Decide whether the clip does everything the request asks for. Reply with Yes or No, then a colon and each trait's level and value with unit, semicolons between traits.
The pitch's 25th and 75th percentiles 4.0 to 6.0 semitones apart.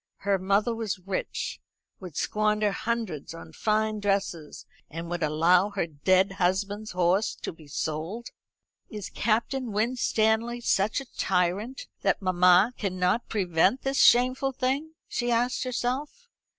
Yes: average, 4.6 semitones